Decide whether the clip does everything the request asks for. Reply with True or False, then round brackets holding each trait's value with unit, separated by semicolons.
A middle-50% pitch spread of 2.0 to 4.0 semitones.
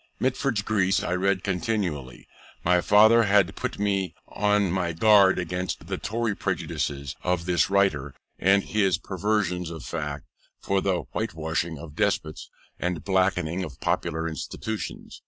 True (3.7 semitones)